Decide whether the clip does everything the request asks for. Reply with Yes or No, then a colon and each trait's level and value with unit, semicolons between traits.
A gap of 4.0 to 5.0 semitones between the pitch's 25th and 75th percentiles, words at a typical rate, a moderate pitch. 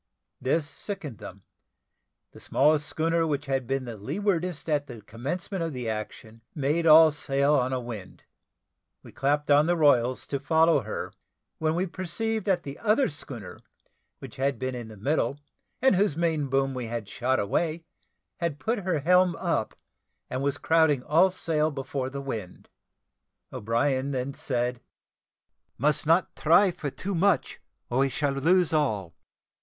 Yes: average, 4.3 semitones; average, 160 wpm; medium, 145 Hz